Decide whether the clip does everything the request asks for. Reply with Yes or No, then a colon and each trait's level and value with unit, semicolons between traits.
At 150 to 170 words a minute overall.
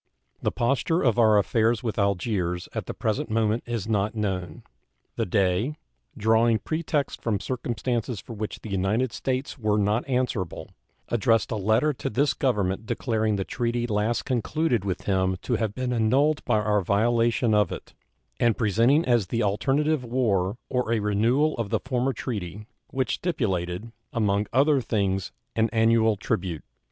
Yes: average, 160 wpm